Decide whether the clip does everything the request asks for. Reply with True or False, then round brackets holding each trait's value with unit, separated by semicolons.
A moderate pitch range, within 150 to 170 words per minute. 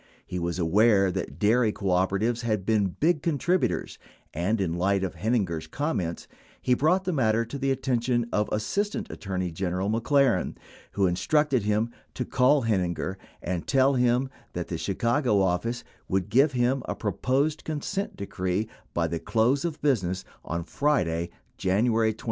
False (6.1 semitones; 155 wpm)